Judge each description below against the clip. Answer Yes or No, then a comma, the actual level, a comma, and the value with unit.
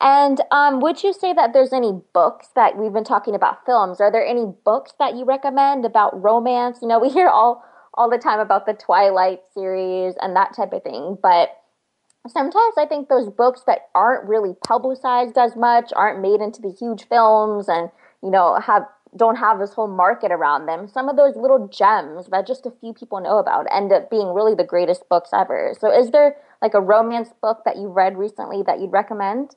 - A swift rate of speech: Yes, fast, 210 wpm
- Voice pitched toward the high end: Yes, high, 220 Hz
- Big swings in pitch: No, average, 4.8 semitones